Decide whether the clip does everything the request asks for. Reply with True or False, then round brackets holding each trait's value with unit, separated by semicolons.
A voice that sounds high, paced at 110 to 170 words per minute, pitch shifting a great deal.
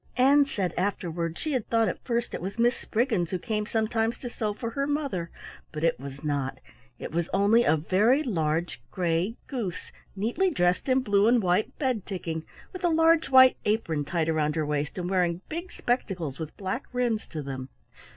False (200 Hz; 195 wpm; 6.6 semitones)